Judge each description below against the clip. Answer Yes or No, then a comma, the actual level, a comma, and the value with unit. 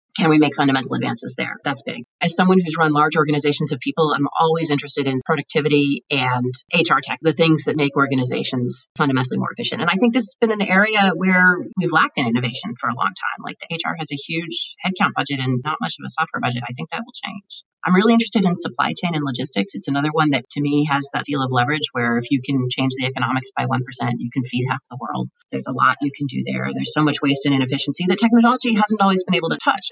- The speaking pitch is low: No, medium, 145 Hz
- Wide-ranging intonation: No, average, 5.0 semitones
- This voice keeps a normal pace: No, fast, 250 wpm